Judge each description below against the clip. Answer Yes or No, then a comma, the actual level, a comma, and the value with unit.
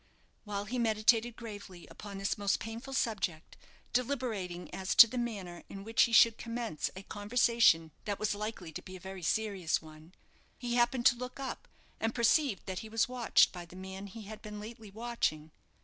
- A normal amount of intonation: Yes, average, 3.7 semitones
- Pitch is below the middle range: No, high, 215 Hz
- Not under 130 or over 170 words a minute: No, average, 185 wpm